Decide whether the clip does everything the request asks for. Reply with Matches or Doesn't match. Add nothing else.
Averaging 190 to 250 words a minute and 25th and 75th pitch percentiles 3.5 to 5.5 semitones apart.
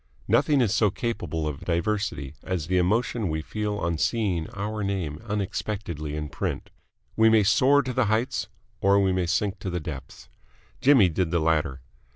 Doesn't match